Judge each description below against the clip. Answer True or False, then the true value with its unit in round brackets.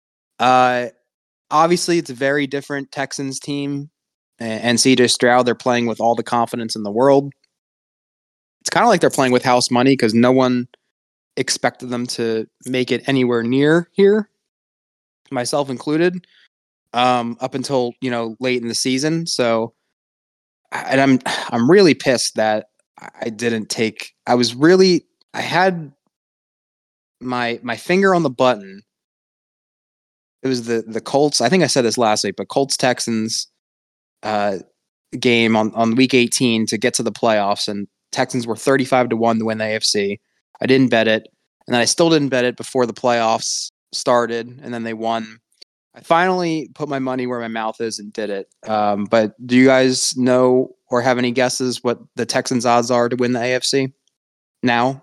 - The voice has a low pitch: True (125 Hz)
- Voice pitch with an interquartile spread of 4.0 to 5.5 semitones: False (2.8 semitones)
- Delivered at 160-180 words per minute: True (175 wpm)